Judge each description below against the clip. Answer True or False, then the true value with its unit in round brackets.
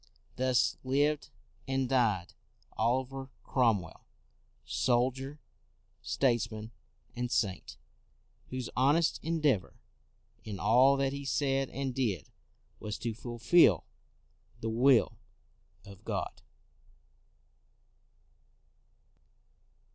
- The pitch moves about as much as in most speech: True (3.2 semitones)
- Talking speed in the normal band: False (85 wpm)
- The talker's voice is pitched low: True (125 Hz)